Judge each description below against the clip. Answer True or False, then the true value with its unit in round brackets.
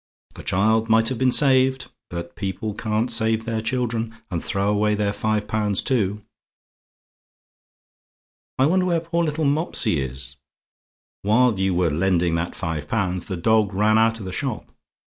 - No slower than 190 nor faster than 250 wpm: False (160 wpm)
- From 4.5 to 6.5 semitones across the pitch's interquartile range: False (3.8 semitones)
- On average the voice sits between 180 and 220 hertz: False (110 Hz)